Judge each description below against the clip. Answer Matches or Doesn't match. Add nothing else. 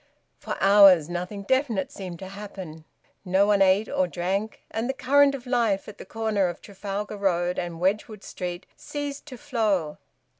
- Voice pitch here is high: Matches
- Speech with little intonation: Doesn't match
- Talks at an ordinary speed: Matches